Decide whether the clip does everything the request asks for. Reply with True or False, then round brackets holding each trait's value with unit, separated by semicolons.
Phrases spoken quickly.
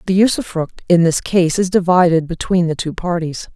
False (185 wpm)